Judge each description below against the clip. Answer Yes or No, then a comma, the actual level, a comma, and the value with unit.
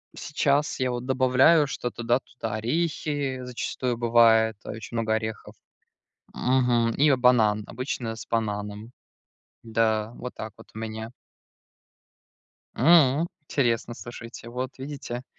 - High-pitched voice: No, low, 120 Hz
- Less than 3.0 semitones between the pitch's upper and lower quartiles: Yes, narrow, 2.6 semitones